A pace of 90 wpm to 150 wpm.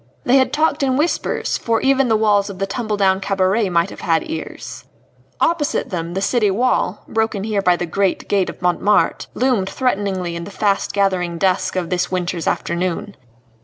No: average, 185 wpm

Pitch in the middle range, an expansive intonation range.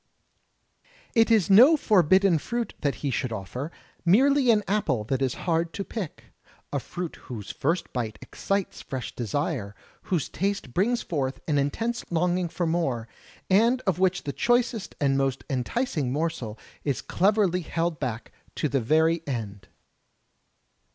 Yes: medium, 165 Hz; wide, 6.8 semitones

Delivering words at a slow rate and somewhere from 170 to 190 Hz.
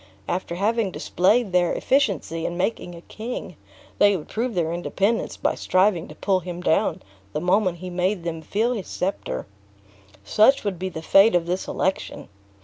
No: average, 170 wpm; medium, 185 Hz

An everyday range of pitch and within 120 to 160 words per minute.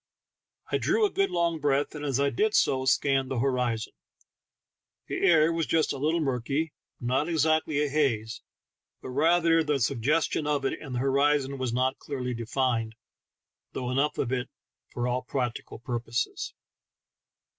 Yes: average, 3.6 semitones; average, 155 wpm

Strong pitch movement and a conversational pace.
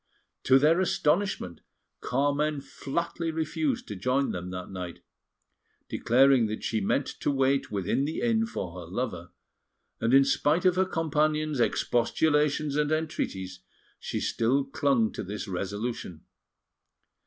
No: wide, 6.0 semitones; slow, 130 wpm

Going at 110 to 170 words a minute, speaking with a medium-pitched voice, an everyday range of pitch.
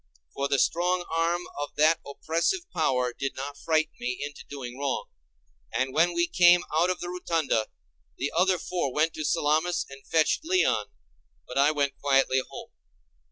Yes: average, 165 wpm; medium, 155 Hz; average, 4.0 semitones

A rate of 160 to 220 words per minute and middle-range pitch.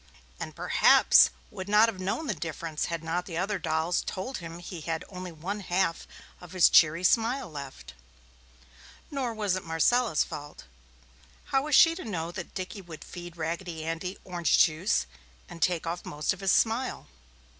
Yes: average, 170 wpm; medium, 180 Hz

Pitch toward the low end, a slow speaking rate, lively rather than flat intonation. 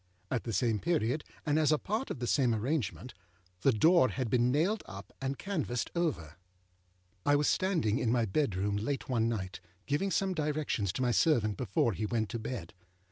No: low, 125 Hz; average, 185 wpm; wide, 6.1 semitones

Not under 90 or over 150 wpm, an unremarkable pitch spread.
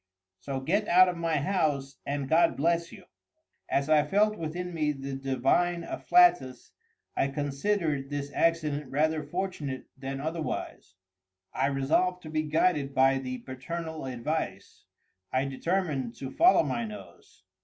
Yes: average, 140 wpm; average, 3.9 semitones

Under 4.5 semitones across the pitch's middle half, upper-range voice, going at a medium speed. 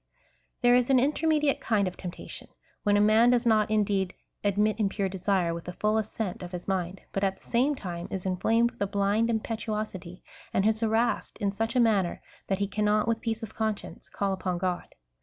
No: average, 2.8 semitones; high, 210 Hz; fast, 210 wpm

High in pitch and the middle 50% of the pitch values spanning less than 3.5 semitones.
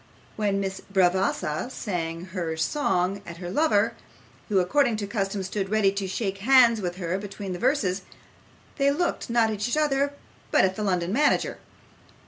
No: high, 200 Hz; average, 4.1 semitones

